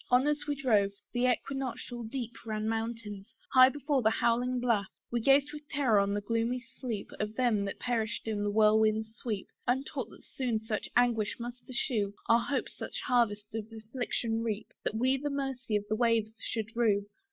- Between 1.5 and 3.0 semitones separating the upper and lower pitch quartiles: Yes, average, 2.7 semitones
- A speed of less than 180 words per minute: No, average, 185 wpm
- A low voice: No, high, 230 Hz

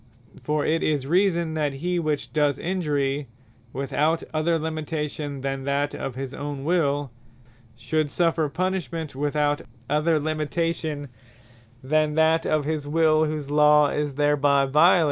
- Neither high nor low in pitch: Yes, medium, 150 Hz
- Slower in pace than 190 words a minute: Yes, slow, 135 wpm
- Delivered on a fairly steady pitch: Yes, narrow, 1.9 semitones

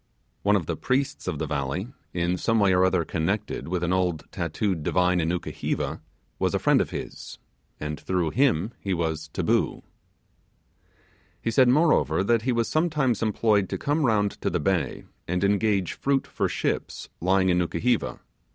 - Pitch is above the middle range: No, very low, 95 Hz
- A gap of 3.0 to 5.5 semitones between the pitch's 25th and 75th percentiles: Yes, average, 4.8 semitones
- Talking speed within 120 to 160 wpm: No, average, 170 wpm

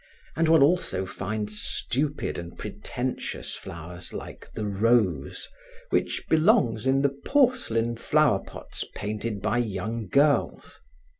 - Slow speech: Yes, slow, 115 wpm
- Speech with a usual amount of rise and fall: No, wide, 5.7 semitones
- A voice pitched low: Yes, low, 115 Hz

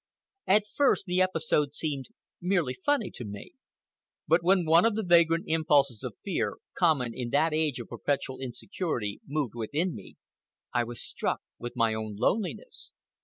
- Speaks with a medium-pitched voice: Yes, medium, 155 Hz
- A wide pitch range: Yes, wide, 6.5 semitones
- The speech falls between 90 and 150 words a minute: No, average, 160 wpm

